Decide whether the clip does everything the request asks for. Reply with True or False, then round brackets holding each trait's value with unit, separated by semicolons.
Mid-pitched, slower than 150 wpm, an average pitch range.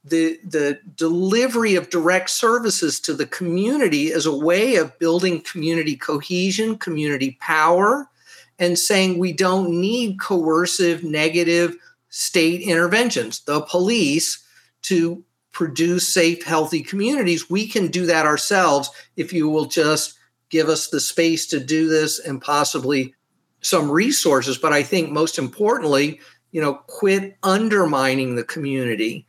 True (170 Hz; 135 wpm; 3.3 semitones)